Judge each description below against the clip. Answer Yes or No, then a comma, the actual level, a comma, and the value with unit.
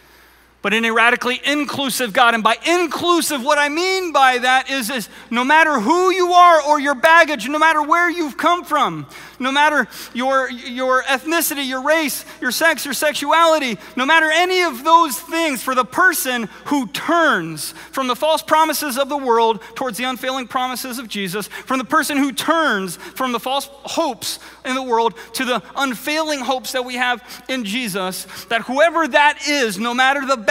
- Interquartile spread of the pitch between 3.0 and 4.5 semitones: Yes, average, 4.1 semitones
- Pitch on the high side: Yes, very high, 270 Hz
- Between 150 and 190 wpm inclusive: Yes, average, 180 wpm